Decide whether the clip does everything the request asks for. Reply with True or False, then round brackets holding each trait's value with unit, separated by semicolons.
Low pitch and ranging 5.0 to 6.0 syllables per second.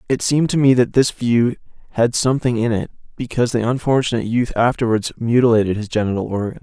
False (120 Hz; 6.4 syllables/s)